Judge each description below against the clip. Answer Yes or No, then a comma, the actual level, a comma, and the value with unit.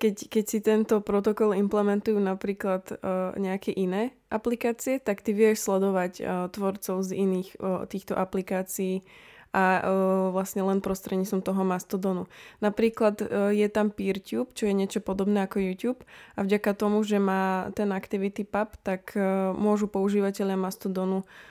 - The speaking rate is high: No, average, 150 wpm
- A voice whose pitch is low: No, high, 200 Hz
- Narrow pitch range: Yes, narrow, 1.8 semitones